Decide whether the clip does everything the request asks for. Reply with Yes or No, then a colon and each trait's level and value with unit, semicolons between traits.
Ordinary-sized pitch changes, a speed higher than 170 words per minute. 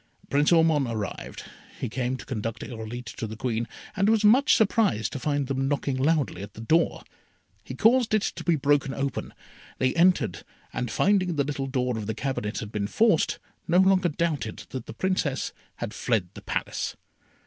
No: wide, 6.8 semitones; average, 180 wpm